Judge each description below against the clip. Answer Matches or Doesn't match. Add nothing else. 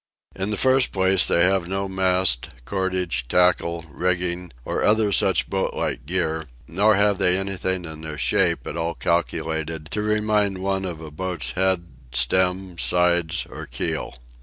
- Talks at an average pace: Matches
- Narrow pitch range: Matches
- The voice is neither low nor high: Doesn't match